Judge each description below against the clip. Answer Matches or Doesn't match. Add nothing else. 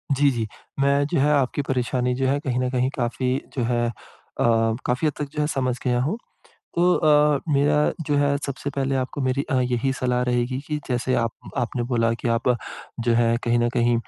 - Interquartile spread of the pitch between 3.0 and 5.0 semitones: Doesn't match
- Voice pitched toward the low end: Matches